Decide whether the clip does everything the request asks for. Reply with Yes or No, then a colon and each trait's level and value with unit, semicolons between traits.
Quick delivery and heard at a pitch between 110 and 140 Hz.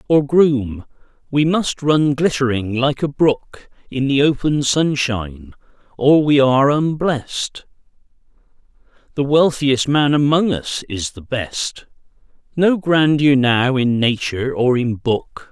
No: slow, 125 wpm; low, 135 Hz